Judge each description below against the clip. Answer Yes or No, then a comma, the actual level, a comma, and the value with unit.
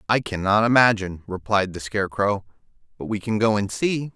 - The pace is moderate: Yes, average, 175 wpm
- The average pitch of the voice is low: Yes, low, 105 Hz